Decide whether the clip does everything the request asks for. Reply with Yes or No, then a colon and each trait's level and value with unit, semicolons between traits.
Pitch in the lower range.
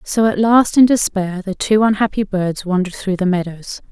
No: high, 200 Hz